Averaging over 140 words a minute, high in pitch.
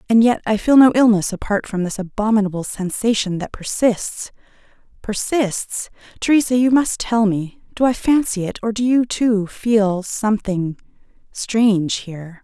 No: slow, 135 wpm; high, 215 Hz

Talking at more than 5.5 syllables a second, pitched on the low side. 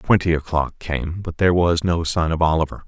No: 5.4 syllables/s; very low, 80 Hz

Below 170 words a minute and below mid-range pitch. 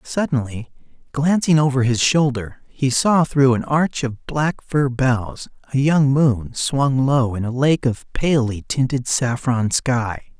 Yes: average, 155 wpm; low, 130 Hz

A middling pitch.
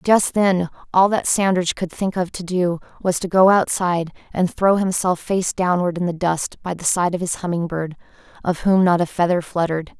Yes: medium, 180 Hz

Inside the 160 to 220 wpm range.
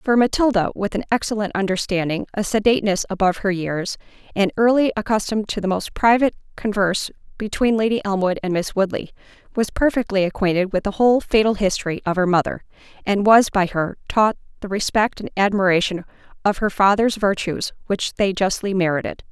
Yes: average, 165 wpm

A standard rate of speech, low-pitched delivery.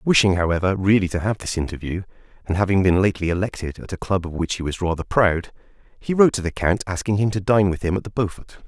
No: fast, 240 wpm; very low, 95 Hz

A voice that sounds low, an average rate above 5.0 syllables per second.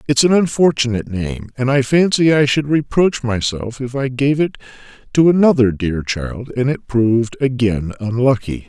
No: low, 130 Hz; 4.8 syllables/s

